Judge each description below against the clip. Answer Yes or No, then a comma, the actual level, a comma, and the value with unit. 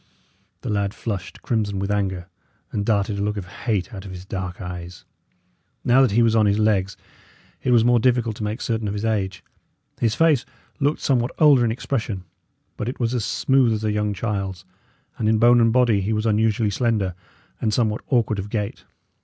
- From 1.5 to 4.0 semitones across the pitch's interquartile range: Yes, average, 2.8 semitones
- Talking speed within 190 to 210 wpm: Yes, average, 200 wpm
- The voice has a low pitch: Yes, low, 110 Hz